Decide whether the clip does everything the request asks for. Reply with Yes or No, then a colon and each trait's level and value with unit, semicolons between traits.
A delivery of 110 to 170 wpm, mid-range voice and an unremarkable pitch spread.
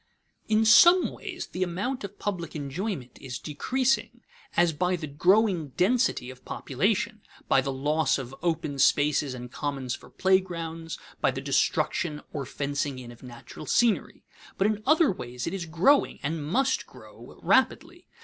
No: average, 155 wpm; medium, 165 Hz; wide, 6.6 semitones